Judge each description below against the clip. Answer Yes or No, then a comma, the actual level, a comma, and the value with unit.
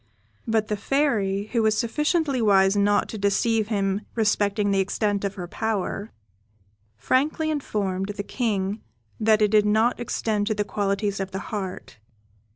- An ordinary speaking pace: Yes, average, 155 wpm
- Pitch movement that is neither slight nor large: No, narrow, 2.1 semitones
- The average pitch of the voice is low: No, high, 210 Hz